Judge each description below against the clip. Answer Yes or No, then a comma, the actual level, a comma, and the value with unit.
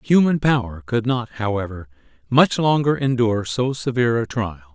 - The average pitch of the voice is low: Yes, low, 120 Hz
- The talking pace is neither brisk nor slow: Yes, average, 150 wpm